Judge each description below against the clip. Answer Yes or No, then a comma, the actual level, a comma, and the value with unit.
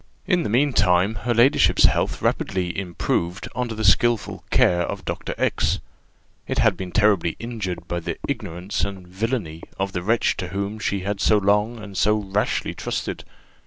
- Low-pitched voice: Yes, low, 100 Hz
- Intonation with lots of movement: No, average, 3.5 semitones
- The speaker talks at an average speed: Yes, average, 165 wpm